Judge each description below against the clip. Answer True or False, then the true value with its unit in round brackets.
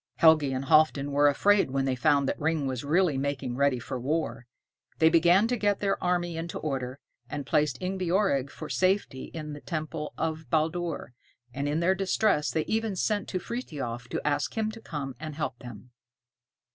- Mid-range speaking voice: True (155 Hz)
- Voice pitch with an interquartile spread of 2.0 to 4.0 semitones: False (4.5 semitones)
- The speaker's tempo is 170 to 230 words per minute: True (185 wpm)